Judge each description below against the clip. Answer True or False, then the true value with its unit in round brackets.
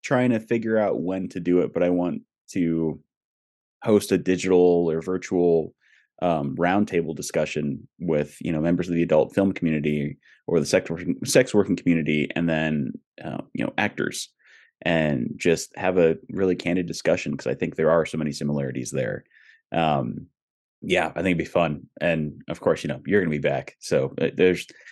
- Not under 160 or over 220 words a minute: True (185 wpm)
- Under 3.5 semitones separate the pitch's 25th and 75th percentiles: True (2.9 semitones)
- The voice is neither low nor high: False (85 Hz)